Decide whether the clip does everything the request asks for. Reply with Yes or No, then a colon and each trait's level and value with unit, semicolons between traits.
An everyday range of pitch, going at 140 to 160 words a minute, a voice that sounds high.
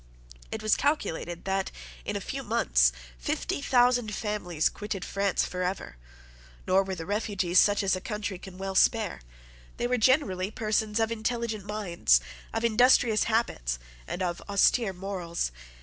Yes: average, 3.4 semitones; average, 150 wpm; high, 200 Hz